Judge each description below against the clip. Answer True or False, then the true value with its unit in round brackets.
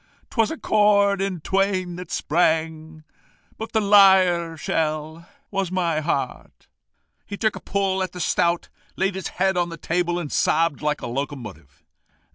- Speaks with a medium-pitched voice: True (175 Hz)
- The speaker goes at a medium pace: True (155 wpm)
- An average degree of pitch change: True (3.5 semitones)